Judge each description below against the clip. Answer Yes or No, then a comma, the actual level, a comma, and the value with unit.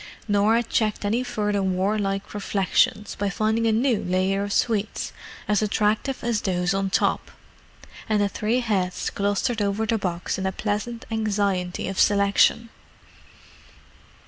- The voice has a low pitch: No, high, 205 Hz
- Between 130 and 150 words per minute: Yes, average, 140 wpm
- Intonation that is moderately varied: No, narrow, 2.0 semitones